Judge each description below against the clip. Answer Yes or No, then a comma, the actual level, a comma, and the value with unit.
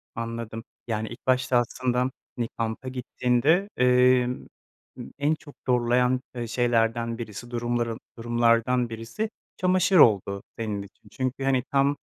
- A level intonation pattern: Yes, narrow, 1.9 semitones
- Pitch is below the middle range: Yes, low, 120 Hz